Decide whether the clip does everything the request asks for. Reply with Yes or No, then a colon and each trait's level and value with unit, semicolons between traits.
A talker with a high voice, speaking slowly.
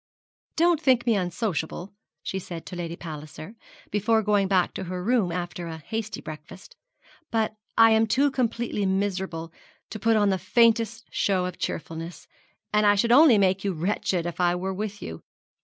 No: high, 195 Hz; average, 175 wpm